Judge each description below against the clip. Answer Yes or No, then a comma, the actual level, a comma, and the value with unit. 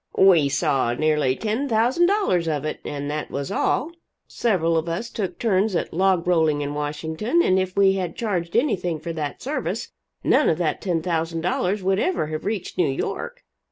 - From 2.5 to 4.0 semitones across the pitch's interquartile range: No, average, 4.6 semitones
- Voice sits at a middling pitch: Yes, medium, 175 Hz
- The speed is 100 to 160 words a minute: No, average, 180 wpm